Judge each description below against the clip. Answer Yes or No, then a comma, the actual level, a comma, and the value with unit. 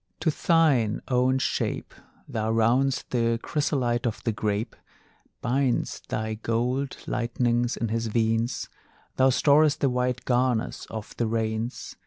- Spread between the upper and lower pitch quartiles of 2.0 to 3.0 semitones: Yes, narrow, 2.5 semitones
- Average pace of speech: No, slow, 130 wpm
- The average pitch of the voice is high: No, low, 120 Hz